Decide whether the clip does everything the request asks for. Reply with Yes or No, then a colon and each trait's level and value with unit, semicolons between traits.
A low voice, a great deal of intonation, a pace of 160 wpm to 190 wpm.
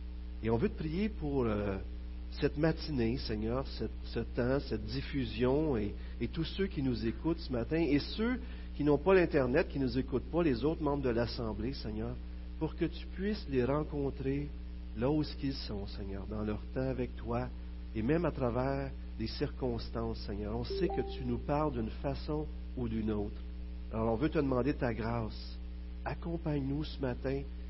Yes: low, 125 Hz; wide, 6.3 semitones; average, 185 wpm